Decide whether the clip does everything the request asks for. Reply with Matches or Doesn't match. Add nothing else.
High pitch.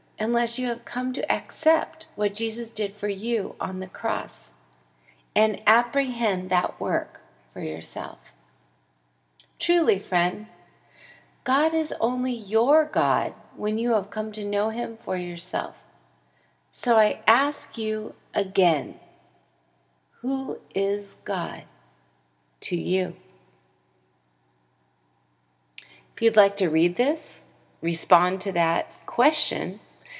Matches